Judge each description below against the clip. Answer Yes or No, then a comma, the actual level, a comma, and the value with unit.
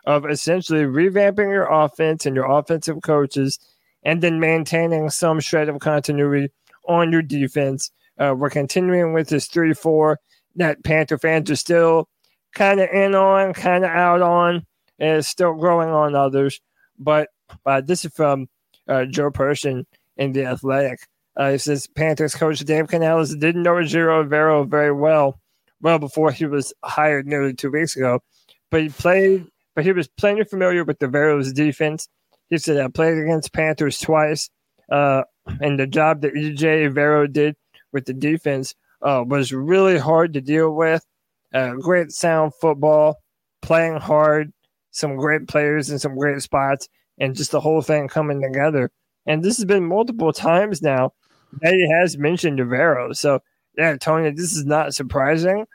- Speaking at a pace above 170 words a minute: No, average, 165 wpm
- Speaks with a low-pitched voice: No, medium, 155 Hz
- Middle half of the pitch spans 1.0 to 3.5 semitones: Yes, narrow, 2.5 semitones